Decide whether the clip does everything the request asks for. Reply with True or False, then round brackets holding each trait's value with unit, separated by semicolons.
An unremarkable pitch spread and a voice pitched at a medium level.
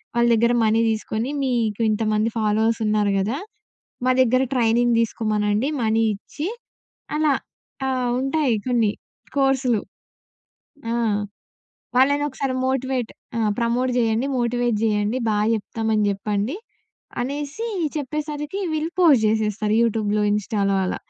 False (3.5 semitones; 230 Hz)